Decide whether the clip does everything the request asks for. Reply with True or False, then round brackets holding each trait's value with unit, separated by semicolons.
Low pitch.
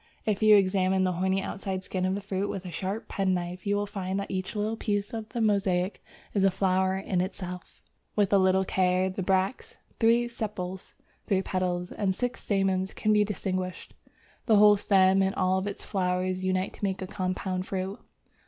False (190 Hz)